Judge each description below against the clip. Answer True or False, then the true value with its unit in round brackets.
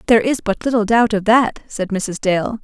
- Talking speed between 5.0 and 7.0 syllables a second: True (5.1 syllables/s)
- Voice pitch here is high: True (215 Hz)